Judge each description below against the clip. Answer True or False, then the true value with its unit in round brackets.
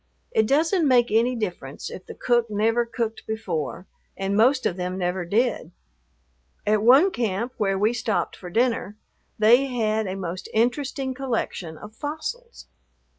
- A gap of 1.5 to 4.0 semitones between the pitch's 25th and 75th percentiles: False (4.4 semitones)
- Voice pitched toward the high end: True (225 Hz)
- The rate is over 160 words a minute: False (150 wpm)